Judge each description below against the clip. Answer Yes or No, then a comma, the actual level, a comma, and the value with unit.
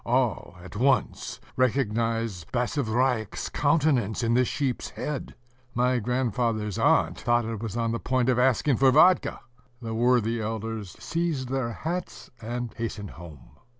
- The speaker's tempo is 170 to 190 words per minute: No, average, 140 wpm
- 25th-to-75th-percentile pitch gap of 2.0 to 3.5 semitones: Yes, narrow, 2.6 semitones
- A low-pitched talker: Yes, low, 120 Hz